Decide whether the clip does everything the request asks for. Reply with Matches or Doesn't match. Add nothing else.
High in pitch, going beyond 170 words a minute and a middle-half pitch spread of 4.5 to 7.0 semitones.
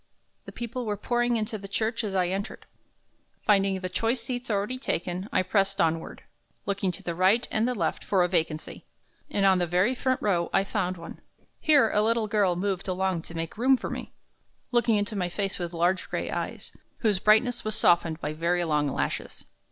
Doesn't match